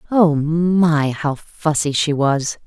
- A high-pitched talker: No, medium, 155 Hz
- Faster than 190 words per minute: No, slow, 135 wpm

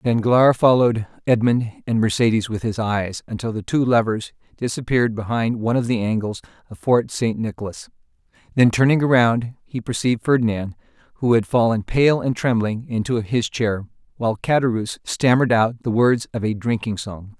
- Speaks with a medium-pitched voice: No, low, 115 Hz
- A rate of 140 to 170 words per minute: Yes, average, 160 wpm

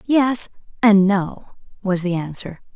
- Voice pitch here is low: No, high, 200 Hz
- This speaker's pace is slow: Yes, slow, 130 wpm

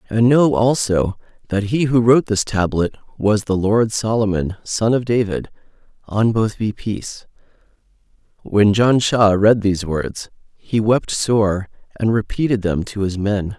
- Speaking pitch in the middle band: No, low, 105 Hz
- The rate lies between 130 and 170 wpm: Yes, average, 150 wpm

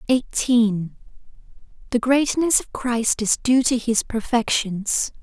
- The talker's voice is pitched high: Yes, high, 235 Hz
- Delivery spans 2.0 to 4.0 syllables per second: Yes, 3.5 syllables/s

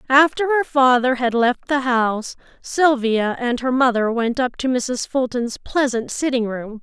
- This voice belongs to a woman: Yes, female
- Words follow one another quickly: No, average, 165 wpm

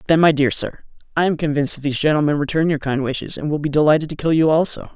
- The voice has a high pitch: No, medium, 150 Hz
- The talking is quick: Yes, fast, 265 wpm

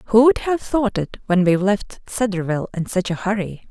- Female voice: Yes, female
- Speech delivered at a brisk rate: Yes, fast, 210 wpm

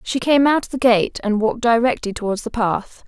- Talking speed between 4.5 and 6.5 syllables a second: Yes, 5.4 syllables/s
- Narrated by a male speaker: No, female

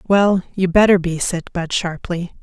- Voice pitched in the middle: Yes, medium, 180 Hz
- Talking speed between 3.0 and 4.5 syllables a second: Yes, 4.2 syllables/s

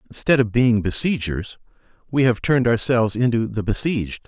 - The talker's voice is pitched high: No, low, 115 Hz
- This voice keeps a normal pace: Yes, average, 155 wpm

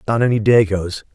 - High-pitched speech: No, low, 105 Hz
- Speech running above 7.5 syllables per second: No, 5.4 syllables/s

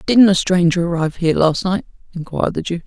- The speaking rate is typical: No, fast, 210 wpm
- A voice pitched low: No, medium, 170 Hz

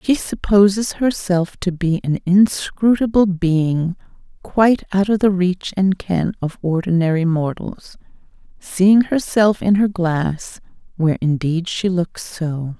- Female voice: Yes, female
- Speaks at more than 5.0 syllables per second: No, 3.8 syllables/s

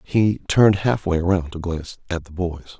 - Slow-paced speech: No, average, 195 wpm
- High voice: No, very low, 90 Hz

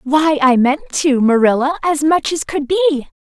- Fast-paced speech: No, average, 185 wpm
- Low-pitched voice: No, very high, 290 Hz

